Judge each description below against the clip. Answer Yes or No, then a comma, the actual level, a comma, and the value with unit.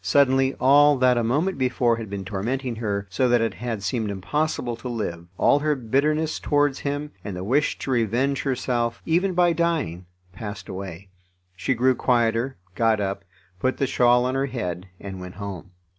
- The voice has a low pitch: Yes, low, 120 Hz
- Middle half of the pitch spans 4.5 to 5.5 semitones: Yes, average, 5.2 semitones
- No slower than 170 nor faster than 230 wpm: Yes, average, 180 wpm